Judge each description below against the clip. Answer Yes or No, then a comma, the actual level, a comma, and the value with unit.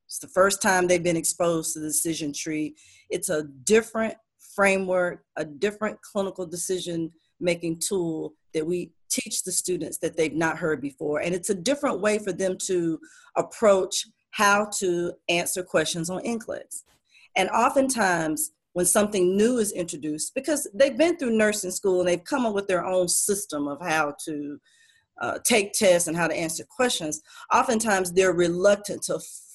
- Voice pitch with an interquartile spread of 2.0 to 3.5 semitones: No, average, 4.3 semitones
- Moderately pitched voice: Yes, medium, 180 Hz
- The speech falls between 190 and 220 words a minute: No, average, 165 wpm